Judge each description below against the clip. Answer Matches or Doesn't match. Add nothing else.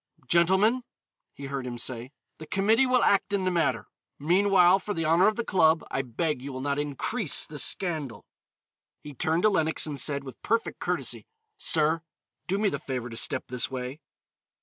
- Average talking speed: Matches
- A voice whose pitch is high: Doesn't match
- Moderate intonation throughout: Doesn't match